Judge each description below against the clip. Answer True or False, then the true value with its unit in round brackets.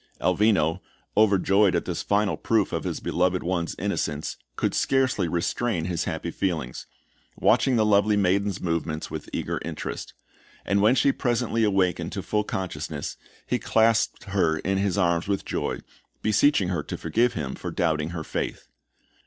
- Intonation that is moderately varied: True (3.9 semitones)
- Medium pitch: False (95 Hz)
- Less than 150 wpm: False (155 wpm)